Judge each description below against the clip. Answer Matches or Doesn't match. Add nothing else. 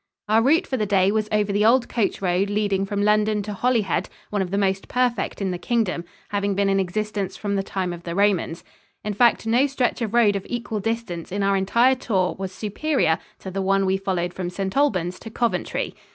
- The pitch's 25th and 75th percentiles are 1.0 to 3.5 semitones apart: Matches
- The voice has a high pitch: Matches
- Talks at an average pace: Doesn't match